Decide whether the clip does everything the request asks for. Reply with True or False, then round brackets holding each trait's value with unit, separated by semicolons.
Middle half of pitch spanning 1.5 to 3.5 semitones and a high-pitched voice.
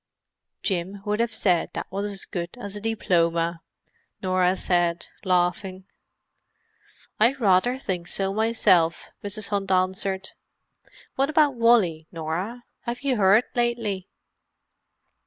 False (4.0 semitones; 195 Hz)